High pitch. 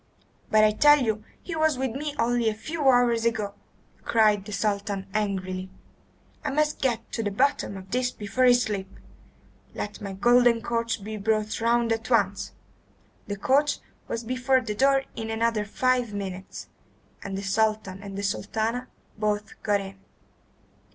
Yes: high, 220 Hz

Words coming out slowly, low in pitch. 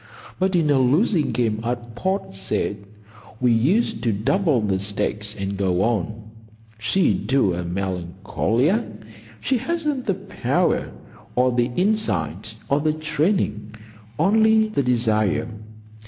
Yes: slow, 125 wpm; low, 120 Hz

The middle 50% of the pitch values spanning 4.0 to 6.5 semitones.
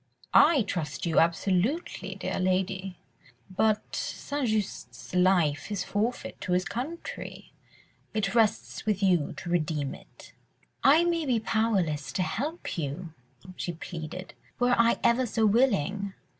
Yes: average, 4.8 semitones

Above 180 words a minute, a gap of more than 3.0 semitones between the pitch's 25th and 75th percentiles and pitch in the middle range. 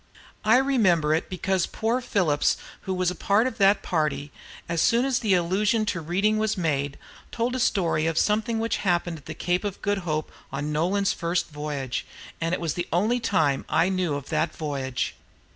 Yes: average, 190 wpm; average, 5.3 semitones; medium, 180 Hz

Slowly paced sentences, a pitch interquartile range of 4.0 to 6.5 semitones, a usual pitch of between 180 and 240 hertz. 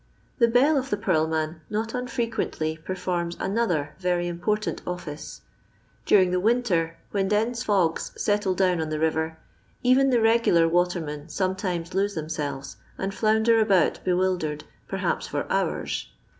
No: average, 145 wpm; average, 5.0 semitones; medium, 185 Hz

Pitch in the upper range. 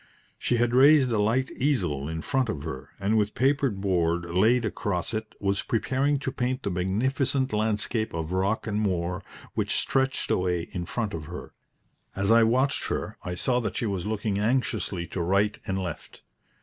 No: low, 105 Hz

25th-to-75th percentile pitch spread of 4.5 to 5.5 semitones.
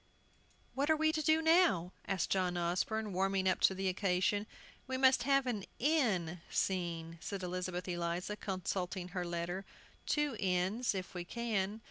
Yes: average, 4.8 semitones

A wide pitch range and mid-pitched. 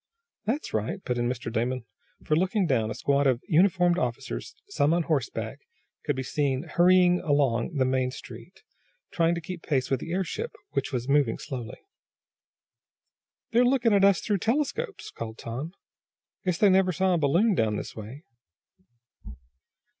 Yes: wide, 6.4 semitones; medium, 150 Hz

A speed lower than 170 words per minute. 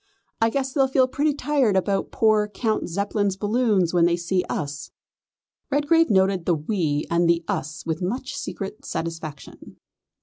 Yes: average, 155 wpm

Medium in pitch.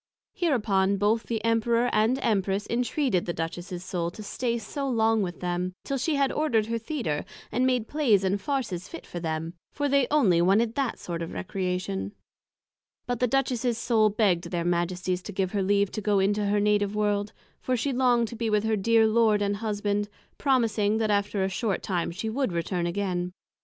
No: high, 210 Hz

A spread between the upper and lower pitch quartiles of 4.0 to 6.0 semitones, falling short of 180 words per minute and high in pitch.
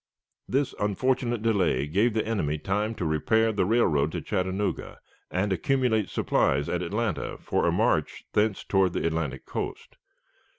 No: average, 4.9 semitones; average, 145 wpm; low, 100 Hz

